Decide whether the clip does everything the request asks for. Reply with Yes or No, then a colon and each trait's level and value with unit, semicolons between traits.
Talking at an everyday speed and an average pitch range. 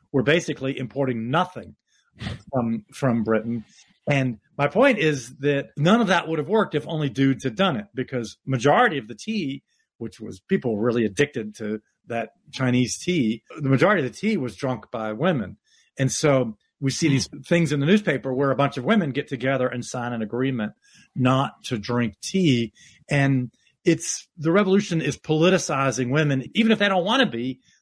Yes: average, 185 wpm; average, 4.8 semitones